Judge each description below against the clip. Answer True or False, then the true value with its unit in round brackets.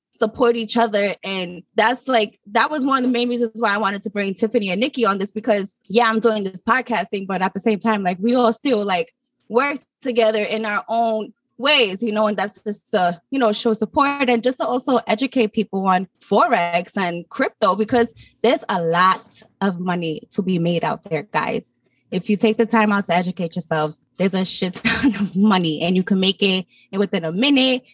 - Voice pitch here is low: False (220 Hz)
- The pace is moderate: False (215 wpm)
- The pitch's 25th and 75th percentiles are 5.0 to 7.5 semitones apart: False (3.5 semitones)